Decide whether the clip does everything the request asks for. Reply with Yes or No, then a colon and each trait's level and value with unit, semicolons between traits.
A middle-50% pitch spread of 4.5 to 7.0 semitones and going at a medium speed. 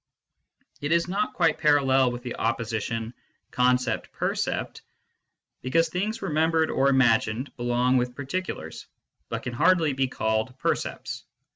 No: average, 4.8 semitones; slow, 130 wpm